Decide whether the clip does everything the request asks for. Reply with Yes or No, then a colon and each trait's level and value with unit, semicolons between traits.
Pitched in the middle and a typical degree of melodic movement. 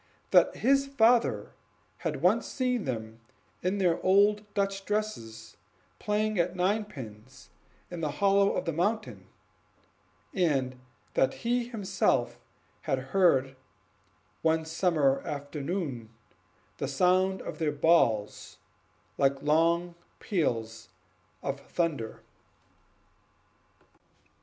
No: medium, 170 Hz; wide, 6.7 semitones